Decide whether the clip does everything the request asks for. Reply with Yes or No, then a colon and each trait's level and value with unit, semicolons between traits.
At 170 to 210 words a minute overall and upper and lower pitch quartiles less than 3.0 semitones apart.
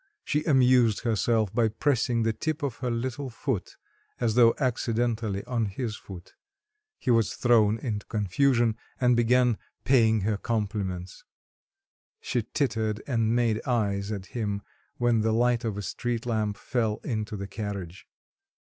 No: average, 145 wpm; narrow, 2.5 semitones